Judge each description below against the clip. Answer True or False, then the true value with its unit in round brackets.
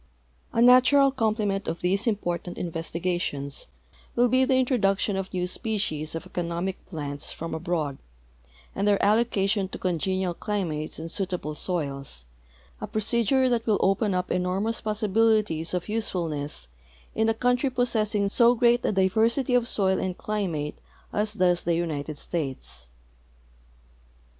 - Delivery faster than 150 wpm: False (135 wpm)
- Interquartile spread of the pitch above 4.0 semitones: True (4.8 semitones)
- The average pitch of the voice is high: True (195 Hz)